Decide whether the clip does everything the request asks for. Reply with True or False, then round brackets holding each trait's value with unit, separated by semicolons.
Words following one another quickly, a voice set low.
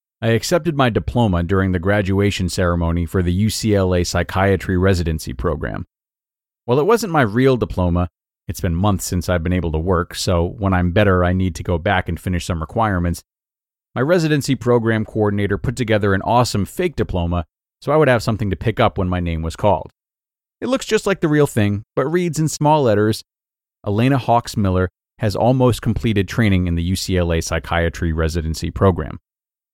False (180 wpm; 100 Hz)